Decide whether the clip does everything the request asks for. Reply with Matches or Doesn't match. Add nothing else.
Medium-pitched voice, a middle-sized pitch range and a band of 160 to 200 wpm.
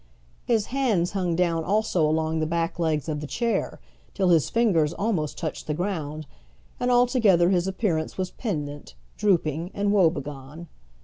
Doesn't match